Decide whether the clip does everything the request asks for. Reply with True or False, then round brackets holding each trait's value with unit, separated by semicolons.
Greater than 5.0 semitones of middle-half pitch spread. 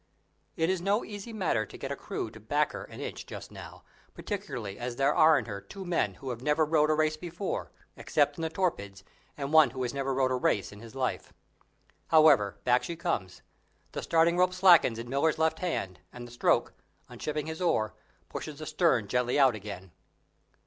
True (5.5 semitones)